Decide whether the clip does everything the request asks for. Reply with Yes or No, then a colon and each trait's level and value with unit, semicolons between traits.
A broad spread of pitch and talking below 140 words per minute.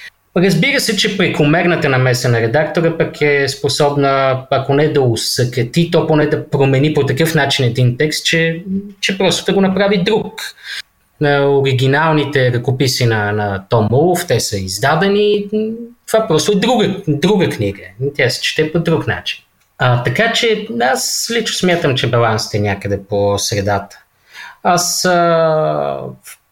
No: wide, 6.7 semitones; average, 145 wpm